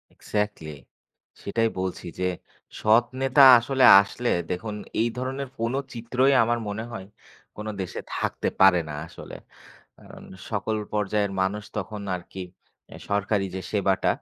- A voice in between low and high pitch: No, low, 105 Hz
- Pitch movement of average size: Yes, average, 3.4 semitones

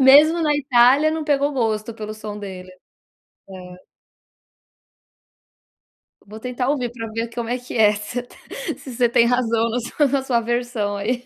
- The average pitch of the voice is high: Yes, high, 240 Hz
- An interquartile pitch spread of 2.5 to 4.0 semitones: Yes, average, 3.4 semitones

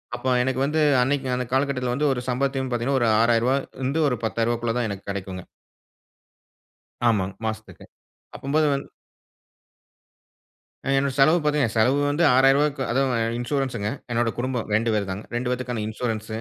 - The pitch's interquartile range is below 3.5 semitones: Yes, average, 3.0 semitones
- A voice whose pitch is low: Yes, low, 125 Hz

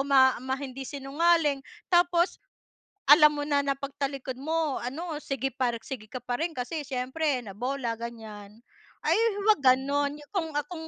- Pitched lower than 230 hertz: No, very high, 275 Hz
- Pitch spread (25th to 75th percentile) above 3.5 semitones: No, average, 3.0 semitones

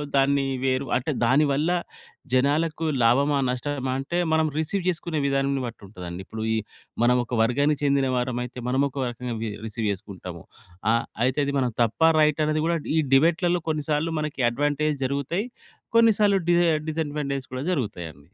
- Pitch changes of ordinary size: Yes, average, 3.7 semitones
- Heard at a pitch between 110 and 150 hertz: Yes, medium, 140 Hz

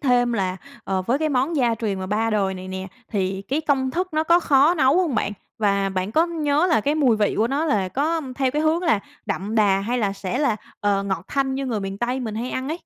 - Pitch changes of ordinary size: No, wide, 6.6 semitones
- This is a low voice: No, high, 240 Hz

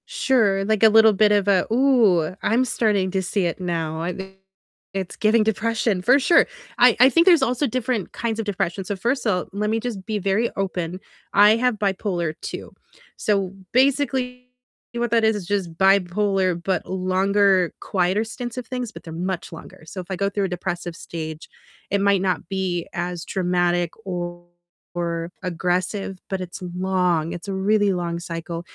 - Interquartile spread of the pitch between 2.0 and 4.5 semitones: Yes, average, 3.6 semitones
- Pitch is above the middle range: Yes, high, 195 Hz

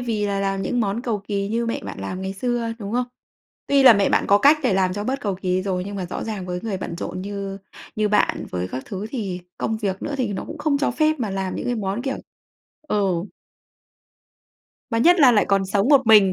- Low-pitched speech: No, high, 205 Hz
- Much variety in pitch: No, average, 3.8 semitones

